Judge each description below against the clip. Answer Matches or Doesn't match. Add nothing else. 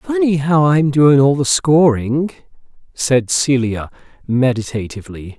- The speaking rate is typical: Doesn't match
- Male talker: Matches